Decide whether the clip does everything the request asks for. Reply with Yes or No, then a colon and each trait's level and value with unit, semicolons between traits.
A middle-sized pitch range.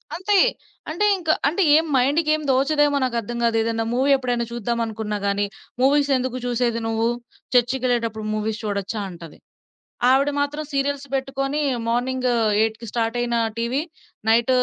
Yes: average, 3.5 semitones